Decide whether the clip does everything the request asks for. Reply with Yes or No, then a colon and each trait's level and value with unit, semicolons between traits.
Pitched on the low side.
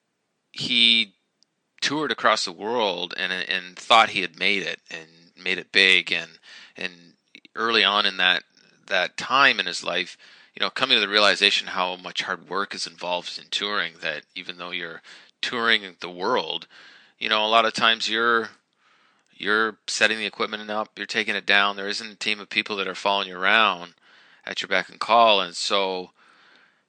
Yes: low, 100 Hz